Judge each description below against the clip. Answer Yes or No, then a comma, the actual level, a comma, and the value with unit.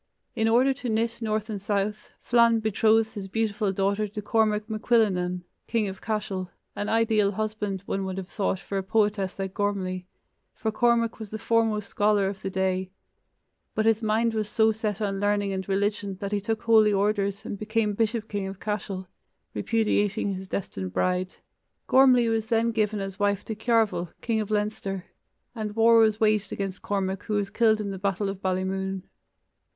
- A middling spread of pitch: No, narrow, 2.2 semitones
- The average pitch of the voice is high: Yes, high, 210 Hz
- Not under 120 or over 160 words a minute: No, average, 180 wpm